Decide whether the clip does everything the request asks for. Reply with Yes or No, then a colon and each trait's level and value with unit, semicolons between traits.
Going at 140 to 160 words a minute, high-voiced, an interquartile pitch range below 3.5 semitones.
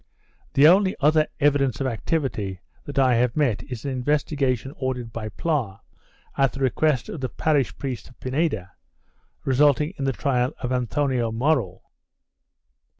No: average, 150 wpm; low, 130 Hz; average, 3.1 semitones